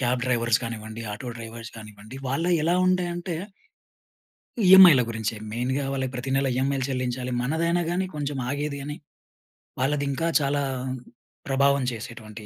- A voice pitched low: Yes, low, 130 Hz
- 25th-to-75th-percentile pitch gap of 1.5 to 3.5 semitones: No, average, 3.9 semitones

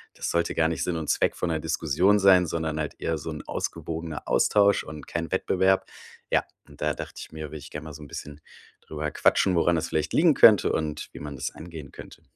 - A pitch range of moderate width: No, narrow, 2.3 semitones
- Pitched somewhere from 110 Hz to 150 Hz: No, very low, 80 Hz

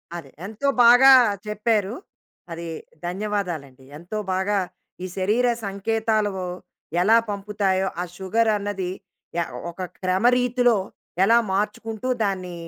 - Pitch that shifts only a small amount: No, average, 3.1 semitones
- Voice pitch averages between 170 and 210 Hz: Yes, high, 205 Hz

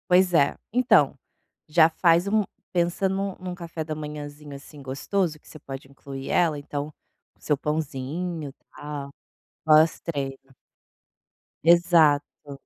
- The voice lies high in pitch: No, medium, 155 Hz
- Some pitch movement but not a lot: Yes, average, 3.3 semitones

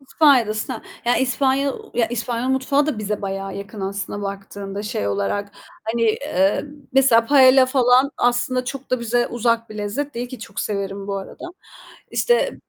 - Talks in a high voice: Yes, high, 235 Hz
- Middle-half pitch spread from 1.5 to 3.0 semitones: No, average, 4.5 semitones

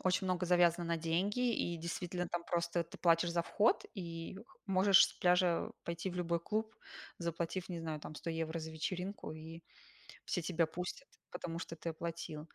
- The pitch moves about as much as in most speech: No, narrow, 1.5 semitones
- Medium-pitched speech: Yes, medium, 170 Hz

